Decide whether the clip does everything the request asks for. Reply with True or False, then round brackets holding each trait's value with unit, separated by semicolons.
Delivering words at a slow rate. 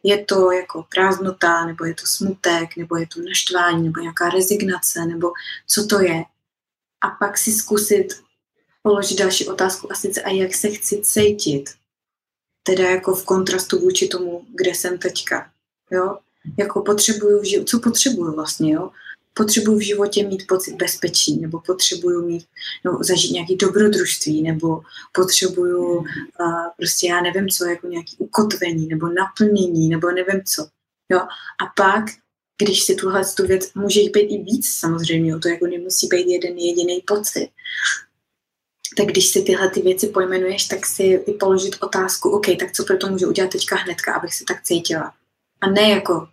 False (165 wpm)